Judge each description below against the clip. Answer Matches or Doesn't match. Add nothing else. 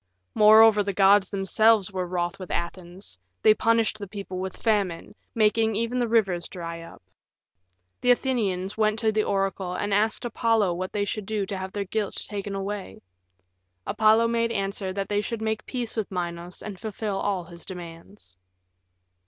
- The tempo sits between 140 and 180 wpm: Matches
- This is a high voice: Matches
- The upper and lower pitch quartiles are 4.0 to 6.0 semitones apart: Doesn't match